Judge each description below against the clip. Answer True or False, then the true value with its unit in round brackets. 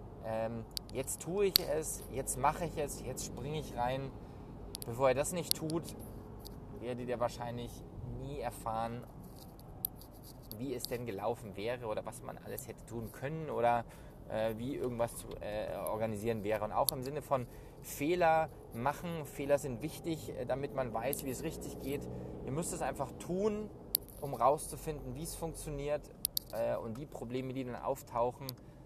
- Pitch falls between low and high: False (125 Hz)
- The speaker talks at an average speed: True (160 wpm)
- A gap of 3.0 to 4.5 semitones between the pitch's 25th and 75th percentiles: True (4.2 semitones)